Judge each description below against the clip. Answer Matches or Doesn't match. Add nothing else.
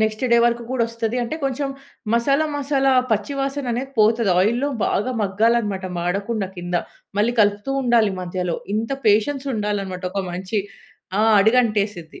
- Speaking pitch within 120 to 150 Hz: Doesn't match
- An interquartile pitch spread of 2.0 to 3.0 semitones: Doesn't match